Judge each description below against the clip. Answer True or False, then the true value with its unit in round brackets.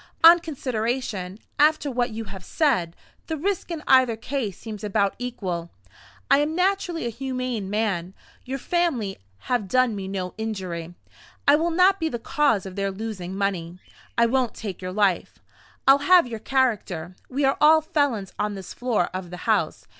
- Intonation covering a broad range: True (6.5 semitones)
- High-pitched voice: True (230 Hz)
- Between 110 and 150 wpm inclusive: False (170 wpm)